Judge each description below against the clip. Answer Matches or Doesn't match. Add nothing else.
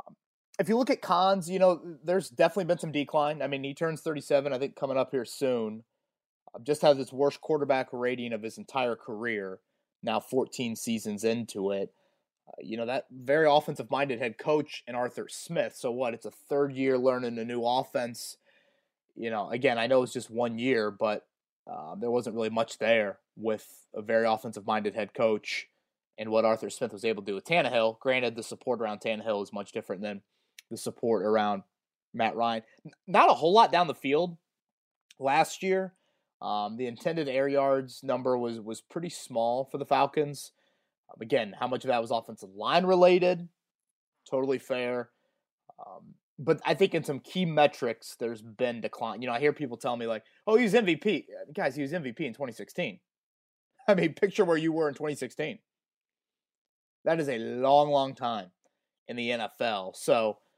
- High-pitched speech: Doesn't match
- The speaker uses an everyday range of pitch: Doesn't match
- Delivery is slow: Doesn't match